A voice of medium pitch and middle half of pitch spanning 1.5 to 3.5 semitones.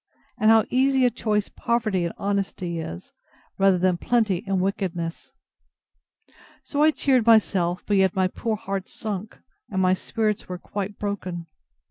No: high, 195 Hz; average, 3.2 semitones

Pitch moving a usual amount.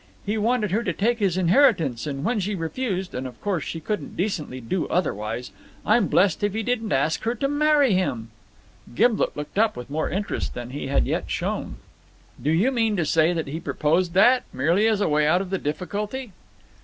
No: wide, 6.4 semitones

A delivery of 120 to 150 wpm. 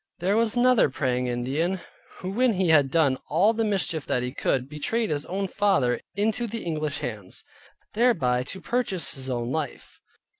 No: average, 175 wpm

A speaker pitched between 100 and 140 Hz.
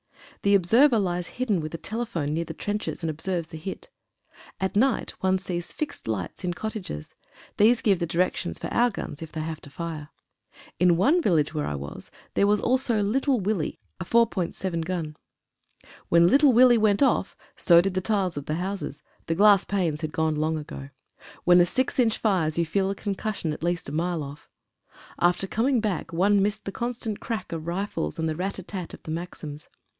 No: medium, 180 Hz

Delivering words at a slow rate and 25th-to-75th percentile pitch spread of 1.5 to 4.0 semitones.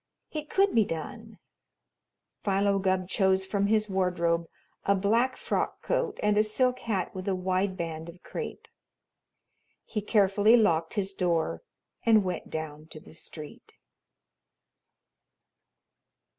Yes: slow, 130 wpm; average, 3.6 semitones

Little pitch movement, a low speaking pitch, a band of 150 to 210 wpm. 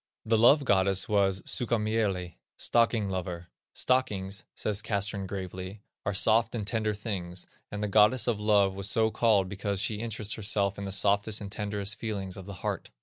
Yes: narrow, 2.1 semitones; low, 100 Hz; average, 170 wpm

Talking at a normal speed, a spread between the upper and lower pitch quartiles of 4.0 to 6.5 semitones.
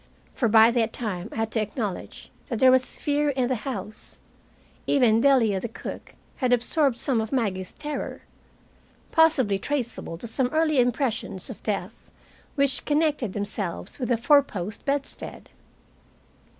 Yes: average, 150 wpm; average, 4.4 semitones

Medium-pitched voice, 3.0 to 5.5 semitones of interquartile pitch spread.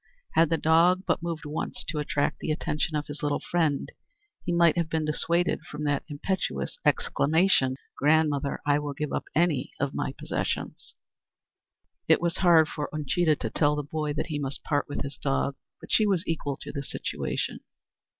No: medium, 150 Hz; narrow, 2.4 semitones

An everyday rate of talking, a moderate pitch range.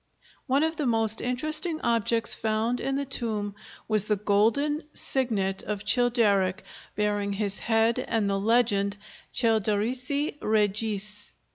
No: slow, 125 wpm; average, 3.1 semitones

